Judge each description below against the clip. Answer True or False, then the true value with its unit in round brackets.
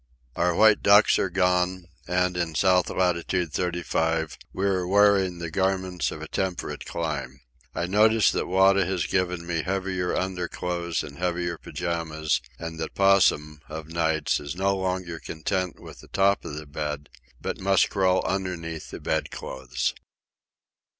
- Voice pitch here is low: True (90 Hz)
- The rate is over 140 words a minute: True (155 wpm)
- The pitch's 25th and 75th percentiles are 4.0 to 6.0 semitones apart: False (2.6 semitones)